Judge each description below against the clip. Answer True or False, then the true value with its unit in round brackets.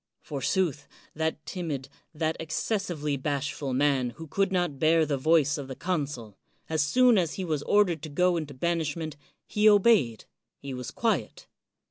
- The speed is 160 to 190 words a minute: False (150 wpm)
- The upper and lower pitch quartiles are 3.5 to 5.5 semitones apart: True (4.0 semitones)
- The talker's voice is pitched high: False (155 Hz)